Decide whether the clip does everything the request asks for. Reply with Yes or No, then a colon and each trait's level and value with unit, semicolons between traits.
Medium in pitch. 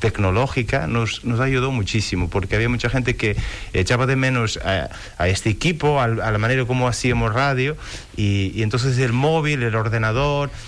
No: low, 115 Hz